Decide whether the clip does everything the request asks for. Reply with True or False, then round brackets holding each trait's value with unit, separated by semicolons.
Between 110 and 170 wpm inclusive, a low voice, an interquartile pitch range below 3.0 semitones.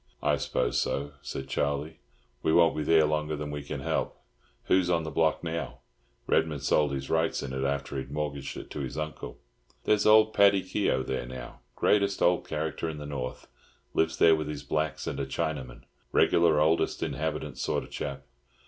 False (185 wpm; 75 Hz; 2.5 semitones)